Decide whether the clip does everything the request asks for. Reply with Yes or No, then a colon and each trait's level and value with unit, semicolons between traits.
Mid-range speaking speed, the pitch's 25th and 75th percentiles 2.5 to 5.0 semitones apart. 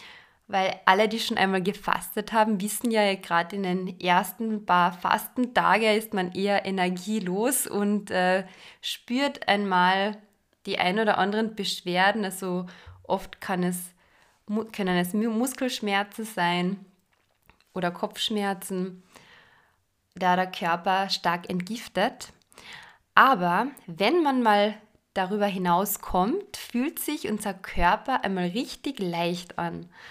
No: slow, 115 wpm; average, 3.1 semitones